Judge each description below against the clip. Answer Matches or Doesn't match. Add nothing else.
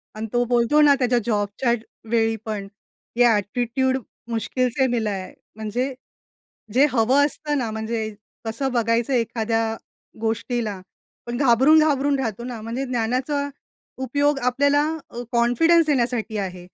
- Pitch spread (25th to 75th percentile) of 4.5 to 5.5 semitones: Doesn't match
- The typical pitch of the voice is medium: Doesn't match